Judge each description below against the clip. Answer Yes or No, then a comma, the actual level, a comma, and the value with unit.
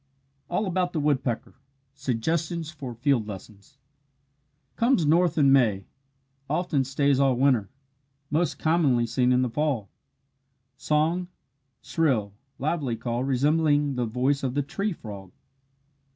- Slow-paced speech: Yes, slow, 125 wpm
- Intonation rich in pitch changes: No, average, 4.3 semitones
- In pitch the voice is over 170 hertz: No, medium, 140 Hz